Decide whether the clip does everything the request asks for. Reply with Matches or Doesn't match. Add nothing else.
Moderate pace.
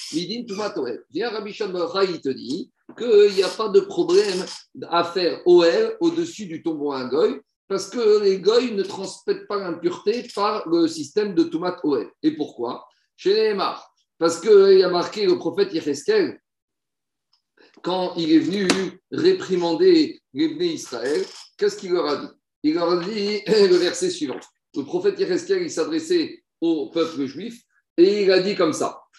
Matches